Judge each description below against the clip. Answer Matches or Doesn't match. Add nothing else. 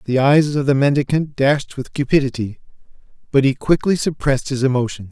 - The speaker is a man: Matches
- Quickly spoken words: Doesn't match